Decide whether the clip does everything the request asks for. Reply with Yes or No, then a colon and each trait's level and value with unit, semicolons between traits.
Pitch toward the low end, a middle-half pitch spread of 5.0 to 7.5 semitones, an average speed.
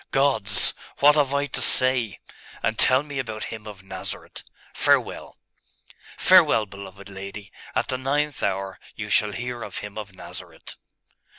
Yes: low, 110 Hz; wide, 5.4 semitones; average, 150 wpm